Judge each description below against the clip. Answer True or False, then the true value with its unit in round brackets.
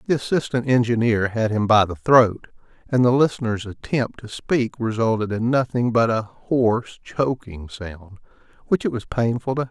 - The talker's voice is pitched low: True (120 Hz)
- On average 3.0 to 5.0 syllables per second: True (4.9 syllables/s)